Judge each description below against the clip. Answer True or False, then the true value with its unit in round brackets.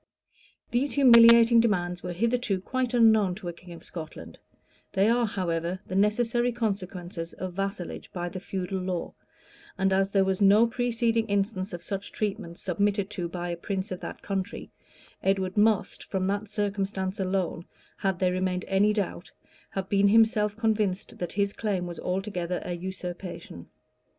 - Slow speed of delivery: False (160 wpm)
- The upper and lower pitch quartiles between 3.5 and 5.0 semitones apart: False (2.8 semitones)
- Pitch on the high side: True (195 Hz)